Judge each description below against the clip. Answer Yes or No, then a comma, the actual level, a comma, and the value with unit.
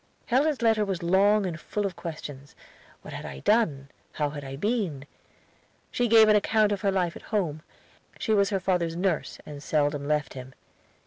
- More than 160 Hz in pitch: Yes, medium, 185 Hz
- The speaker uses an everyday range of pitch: No, wide, 6.0 semitones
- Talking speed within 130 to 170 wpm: No, average, 185 wpm